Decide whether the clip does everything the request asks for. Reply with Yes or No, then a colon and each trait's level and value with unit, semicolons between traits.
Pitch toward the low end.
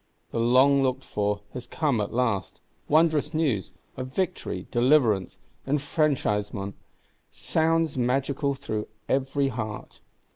Yes: low, 130 Hz